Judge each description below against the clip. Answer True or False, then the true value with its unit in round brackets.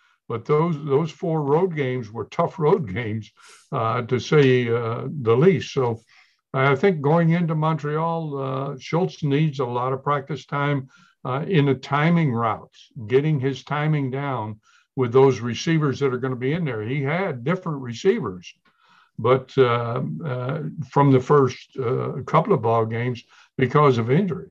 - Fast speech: False (165 wpm)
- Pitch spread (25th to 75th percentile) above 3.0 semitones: True (3.8 semitones)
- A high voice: False (140 Hz)